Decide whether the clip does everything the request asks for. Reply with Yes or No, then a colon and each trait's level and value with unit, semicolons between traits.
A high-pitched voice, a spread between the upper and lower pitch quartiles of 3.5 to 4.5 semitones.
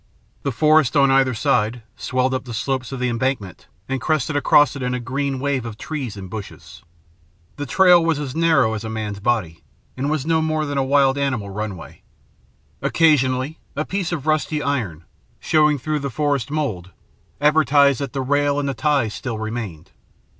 No: low, 135 Hz; average, 4.1 semitones